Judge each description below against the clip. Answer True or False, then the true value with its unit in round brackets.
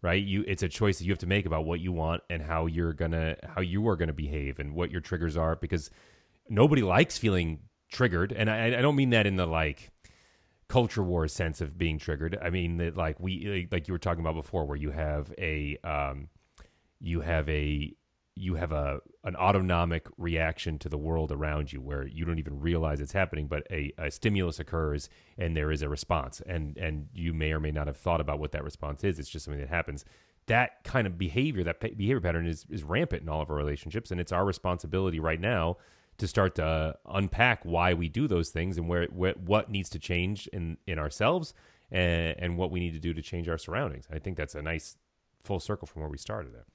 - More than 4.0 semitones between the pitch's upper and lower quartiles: False (3.3 semitones)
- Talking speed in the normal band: False (225 wpm)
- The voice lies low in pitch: True (85 Hz)